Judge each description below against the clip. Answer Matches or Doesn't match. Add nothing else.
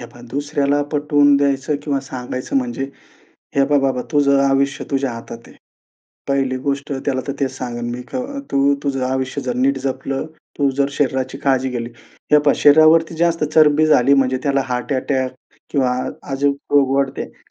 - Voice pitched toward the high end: Doesn't match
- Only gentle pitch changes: Matches